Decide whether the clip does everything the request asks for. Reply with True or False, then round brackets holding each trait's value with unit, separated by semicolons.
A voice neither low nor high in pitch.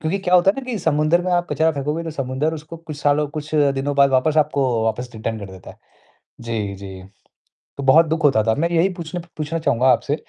True (150 Hz)